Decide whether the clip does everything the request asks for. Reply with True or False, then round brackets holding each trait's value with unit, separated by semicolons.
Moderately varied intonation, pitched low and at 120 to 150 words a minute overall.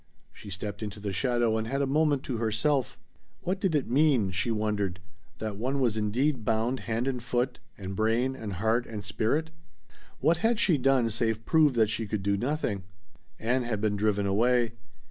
False (4.0 semitones; 115 Hz; 185 wpm)